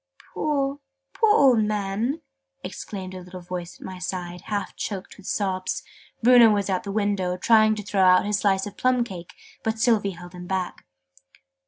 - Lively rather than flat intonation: No, average, 3.2 semitones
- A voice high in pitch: Yes, high, 200 Hz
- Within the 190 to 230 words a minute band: No, average, 175 wpm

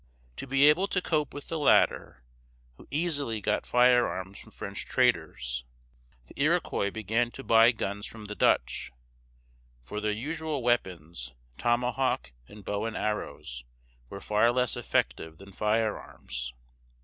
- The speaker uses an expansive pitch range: No, average, 4.5 semitones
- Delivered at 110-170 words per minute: Yes, slow, 135 wpm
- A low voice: Yes, low, 110 Hz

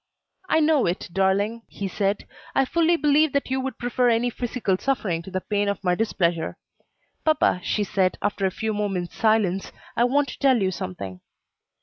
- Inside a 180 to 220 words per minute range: Yes, average, 185 wpm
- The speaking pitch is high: Yes, high, 210 Hz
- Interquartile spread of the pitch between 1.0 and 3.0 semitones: No, wide, 5.5 semitones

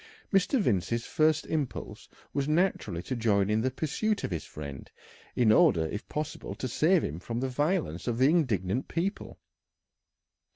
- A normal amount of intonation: No, wide, 7.7 semitones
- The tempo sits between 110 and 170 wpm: Yes, average, 160 wpm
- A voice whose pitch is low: Yes, low, 130 Hz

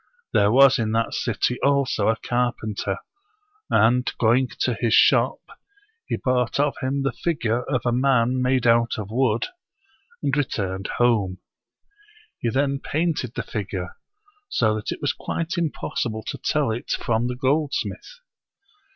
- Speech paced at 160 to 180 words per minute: No, average, 145 wpm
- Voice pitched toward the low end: Yes, low, 125 Hz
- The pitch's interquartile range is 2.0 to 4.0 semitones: Yes, average, 3.6 semitones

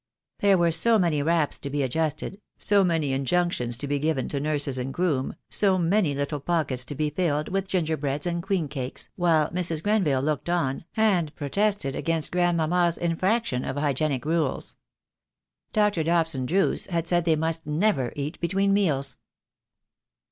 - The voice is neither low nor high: Yes, medium, 160 Hz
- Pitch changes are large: No, average, 3.8 semitones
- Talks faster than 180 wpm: No, average, 160 wpm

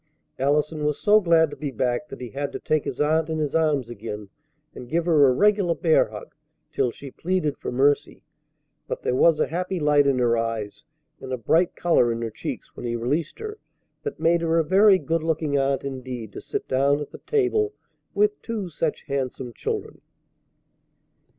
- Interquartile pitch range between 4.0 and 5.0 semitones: Yes, average, 4.6 semitones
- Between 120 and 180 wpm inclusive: No, average, 195 wpm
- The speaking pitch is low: No, medium, 150 Hz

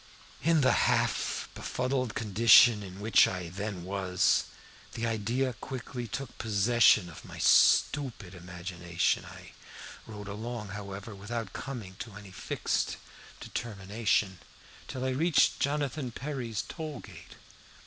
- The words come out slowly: Yes, slow, 120 wpm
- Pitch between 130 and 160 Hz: No, low, 110 Hz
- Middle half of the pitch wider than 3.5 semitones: Yes, average, 4.5 semitones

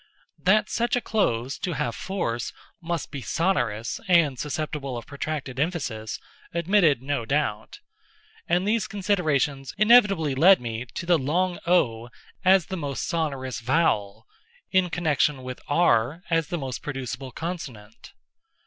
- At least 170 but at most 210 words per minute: No, slow, 135 wpm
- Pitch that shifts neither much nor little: No, wide, 5.8 semitones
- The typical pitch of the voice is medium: Yes, medium, 150 Hz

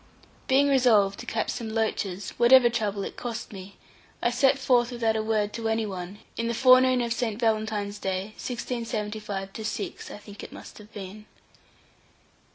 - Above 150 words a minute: Yes, average, 165 wpm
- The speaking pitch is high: Yes, high, 220 Hz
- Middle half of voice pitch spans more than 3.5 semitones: No, average, 2.7 semitones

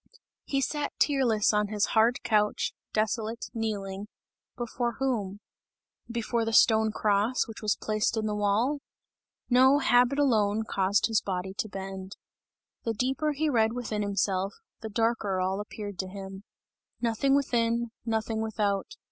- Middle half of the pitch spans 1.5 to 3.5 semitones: Yes, average, 2.8 semitones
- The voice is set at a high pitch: Yes, high, 220 Hz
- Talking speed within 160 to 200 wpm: No, average, 140 wpm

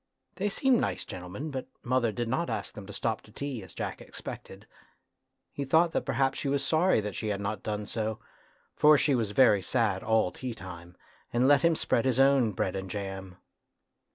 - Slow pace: No, fast, 205 wpm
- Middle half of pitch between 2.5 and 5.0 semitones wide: No, wide, 5.4 semitones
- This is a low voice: Yes, low, 115 Hz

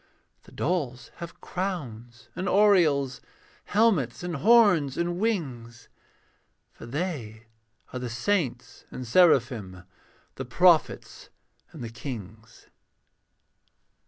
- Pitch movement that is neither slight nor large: No, wide, 7.2 semitones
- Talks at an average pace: No, slow, 100 wpm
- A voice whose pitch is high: No, medium, 140 Hz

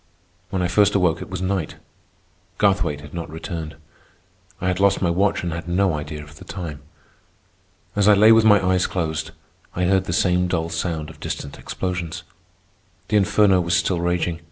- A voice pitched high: No, very low, 90 Hz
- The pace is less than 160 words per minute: No, average, 180 wpm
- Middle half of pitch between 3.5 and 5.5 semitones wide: No, average, 2.7 semitones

